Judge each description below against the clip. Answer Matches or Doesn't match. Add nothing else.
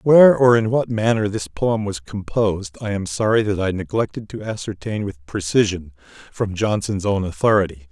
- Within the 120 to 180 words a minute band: Matches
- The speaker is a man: Matches